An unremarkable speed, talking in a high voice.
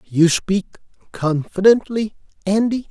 No: slow, 85 wpm; high, 195 Hz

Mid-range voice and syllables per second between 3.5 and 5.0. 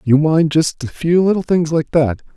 Yes: medium, 155 Hz; 4.8 syllables/s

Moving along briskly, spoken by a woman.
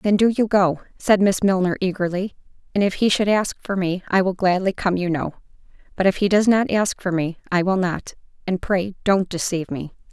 Yes: fast, 215 wpm; female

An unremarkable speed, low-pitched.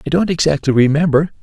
No: average, 170 wpm; medium, 155 Hz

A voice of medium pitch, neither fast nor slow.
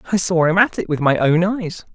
No: medium, 175 Hz; fast, 275 wpm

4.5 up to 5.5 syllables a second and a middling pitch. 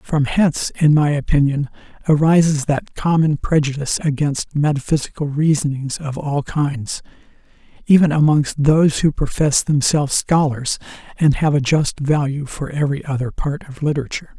Yes: 5.1 syllables/s; medium, 145 Hz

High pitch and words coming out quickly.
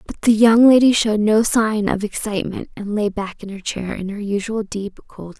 Yes: high, 210 Hz; fast, 235 wpm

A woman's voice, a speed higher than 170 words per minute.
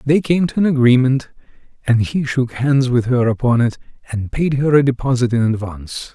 No: male; average, 195 wpm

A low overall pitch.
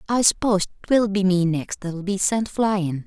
No: high, 195 Hz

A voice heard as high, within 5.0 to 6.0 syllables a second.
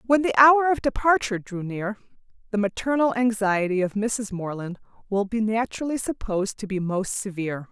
Yes: high, 220 Hz; 5.3 syllables/s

